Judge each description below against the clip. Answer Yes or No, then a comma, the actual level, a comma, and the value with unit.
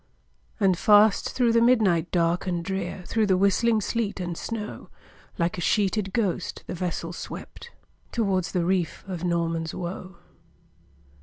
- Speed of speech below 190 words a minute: Yes, average, 145 wpm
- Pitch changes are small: No, average, 3.5 semitones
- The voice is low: No, high, 190 Hz